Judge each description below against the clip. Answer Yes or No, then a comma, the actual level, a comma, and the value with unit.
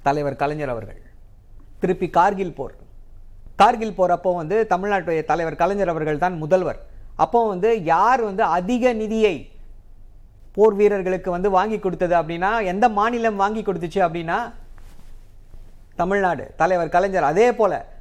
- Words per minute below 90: No, average, 125 wpm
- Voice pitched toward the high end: No, medium, 180 Hz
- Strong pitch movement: Yes, wide, 6.7 semitones